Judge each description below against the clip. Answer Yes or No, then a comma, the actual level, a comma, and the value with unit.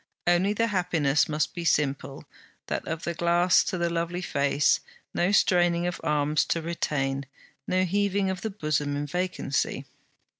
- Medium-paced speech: Yes, average, 155 wpm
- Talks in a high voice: No, medium, 170 Hz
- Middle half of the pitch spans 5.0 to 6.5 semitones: No, average, 3.5 semitones